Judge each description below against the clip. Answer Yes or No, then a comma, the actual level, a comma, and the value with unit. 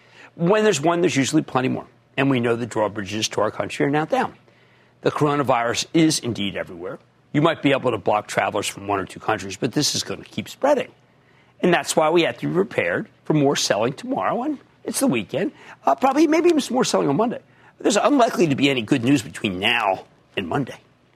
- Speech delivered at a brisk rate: Yes, fast, 220 wpm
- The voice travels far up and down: Yes, wide, 7.6 semitones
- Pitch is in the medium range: Yes, medium, 145 Hz